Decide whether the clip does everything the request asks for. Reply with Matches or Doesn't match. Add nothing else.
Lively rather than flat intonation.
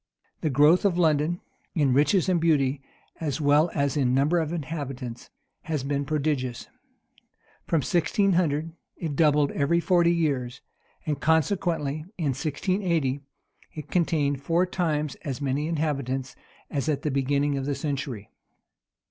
Doesn't match